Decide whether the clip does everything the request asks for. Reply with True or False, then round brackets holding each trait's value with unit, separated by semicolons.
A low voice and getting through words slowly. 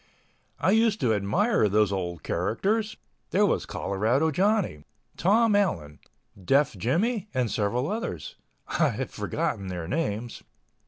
True (125 Hz; 125 wpm)